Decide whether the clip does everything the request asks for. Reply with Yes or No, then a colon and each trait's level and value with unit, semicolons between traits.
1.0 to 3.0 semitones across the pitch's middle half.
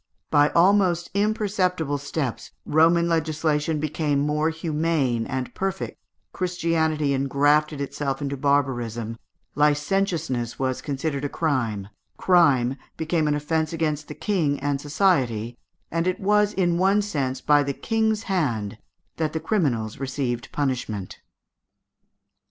No: average, 3.8 semitones